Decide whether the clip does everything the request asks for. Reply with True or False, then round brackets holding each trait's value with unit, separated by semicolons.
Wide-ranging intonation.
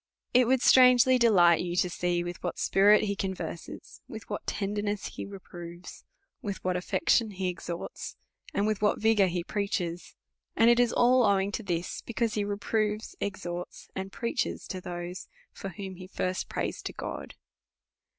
False (3.3 semitones)